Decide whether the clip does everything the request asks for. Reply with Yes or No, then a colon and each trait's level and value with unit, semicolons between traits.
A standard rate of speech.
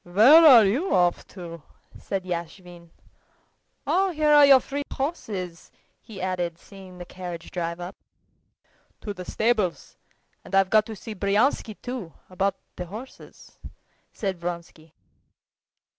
No: slow, 130 wpm